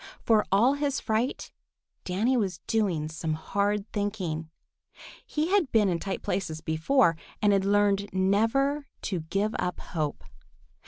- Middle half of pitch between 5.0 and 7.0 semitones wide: No, average, 4.1 semitones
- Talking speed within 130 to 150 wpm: Yes, average, 140 wpm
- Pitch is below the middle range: No, high, 200 Hz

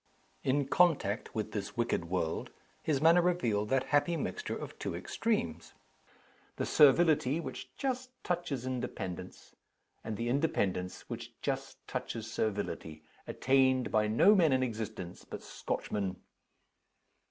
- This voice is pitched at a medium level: No, low, 130 Hz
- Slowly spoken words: Yes, slow, 125 wpm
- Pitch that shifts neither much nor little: No, wide, 7.8 semitones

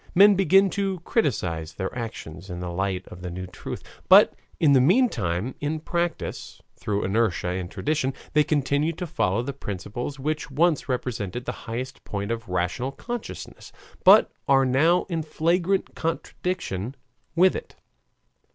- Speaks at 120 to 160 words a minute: Yes, average, 150 wpm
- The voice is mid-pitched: No, low, 130 Hz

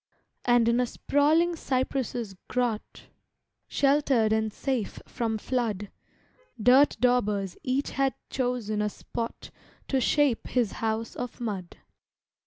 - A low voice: No, high, 240 Hz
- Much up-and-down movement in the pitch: No, average, 3.2 semitones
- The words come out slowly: Yes, slow, 115 wpm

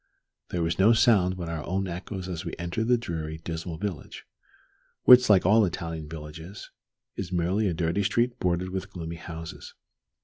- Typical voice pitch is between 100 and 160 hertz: No, very low, 90 Hz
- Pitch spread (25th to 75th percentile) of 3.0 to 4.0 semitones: Yes, average, 3.4 semitones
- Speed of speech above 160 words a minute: Yes, average, 170 wpm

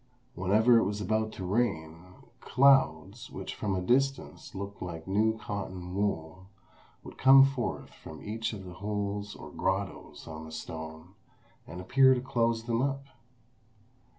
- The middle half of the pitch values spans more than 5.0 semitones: No, average, 4.3 semitones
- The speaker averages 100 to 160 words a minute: Yes, average, 150 wpm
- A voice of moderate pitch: No, low, 100 Hz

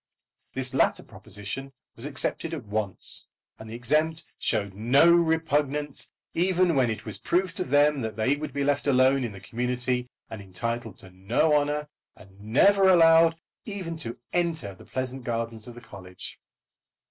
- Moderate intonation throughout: No, wide, 6.1 semitones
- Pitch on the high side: No, low, 130 Hz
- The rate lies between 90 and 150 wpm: No, average, 160 wpm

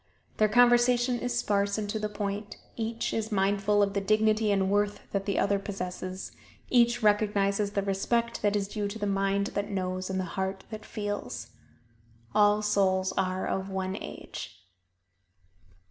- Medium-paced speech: Yes, average, 160 wpm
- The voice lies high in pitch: Yes, high, 205 Hz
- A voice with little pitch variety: Yes, narrow, 1.6 semitones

